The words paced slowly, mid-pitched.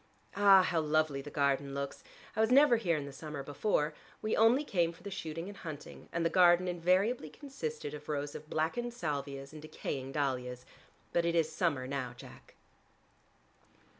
No: average, 175 wpm; medium, 160 Hz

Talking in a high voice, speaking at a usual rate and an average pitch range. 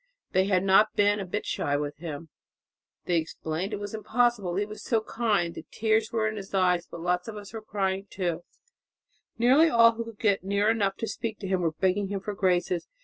No: high, 200 Hz; fast, 215 wpm; average, 3.3 semitones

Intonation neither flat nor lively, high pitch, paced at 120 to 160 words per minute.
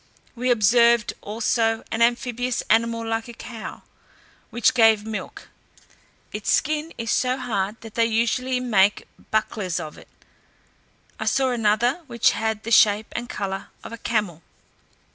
No: narrow, 2.0 semitones; high, 230 Hz; average, 145 wpm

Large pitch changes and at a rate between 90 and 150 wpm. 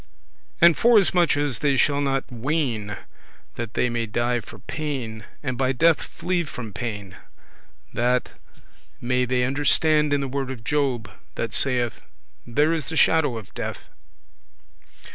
No: average, 3.8 semitones; average, 145 wpm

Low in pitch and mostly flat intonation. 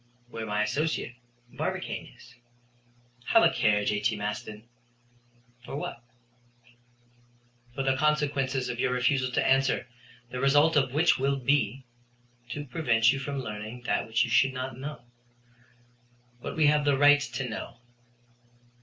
No: low, 130 Hz; average, 3.1 semitones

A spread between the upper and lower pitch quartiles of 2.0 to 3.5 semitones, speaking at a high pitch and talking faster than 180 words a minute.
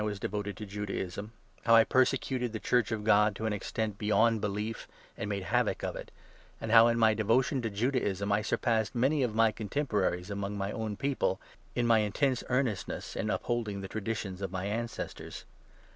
No: narrow, 2.5 semitones; low, 110 Hz; average, 195 wpm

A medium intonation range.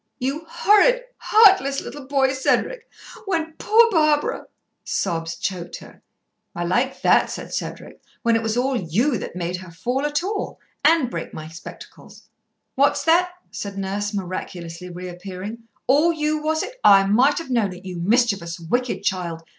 No: wide, 8.7 semitones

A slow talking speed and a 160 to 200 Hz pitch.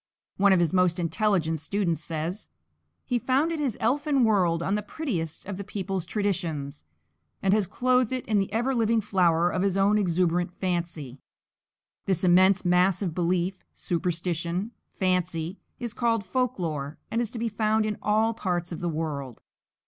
No: average, 165 wpm; high, 190 Hz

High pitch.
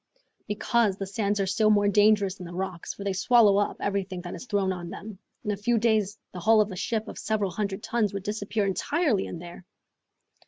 Yes: high, 205 Hz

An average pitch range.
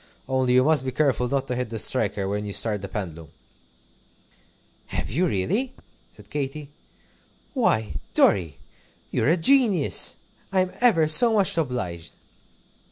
No: wide, 8.0 semitones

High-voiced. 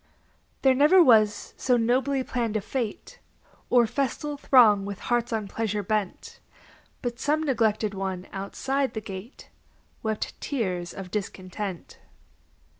Yes: high, 225 Hz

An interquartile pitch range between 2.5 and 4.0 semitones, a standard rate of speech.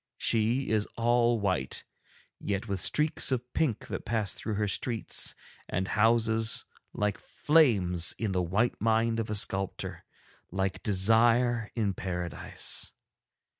No: average, 3.2 semitones; slow, 130 wpm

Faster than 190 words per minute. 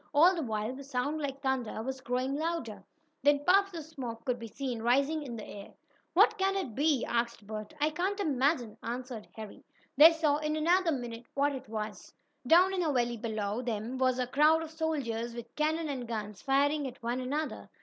Yes: average, 200 wpm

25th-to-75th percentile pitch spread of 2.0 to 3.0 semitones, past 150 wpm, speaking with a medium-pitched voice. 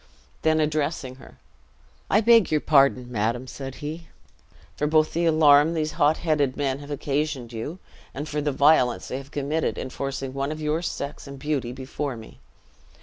Yes: narrow, 2.5 semitones; average, 175 wpm; medium, 145 Hz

